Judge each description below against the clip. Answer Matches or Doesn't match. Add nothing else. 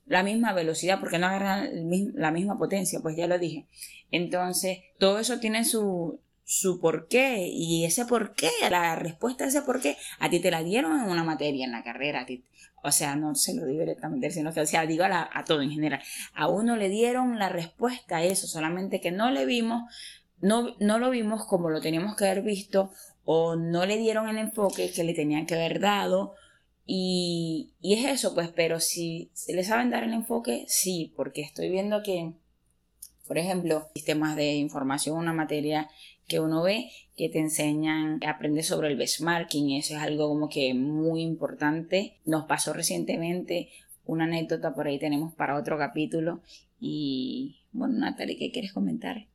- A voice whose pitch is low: Doesn't match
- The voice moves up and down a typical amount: Matches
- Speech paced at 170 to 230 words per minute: Matches